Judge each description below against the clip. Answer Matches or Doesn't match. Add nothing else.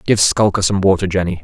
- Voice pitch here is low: Matches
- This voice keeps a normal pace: Doesn't match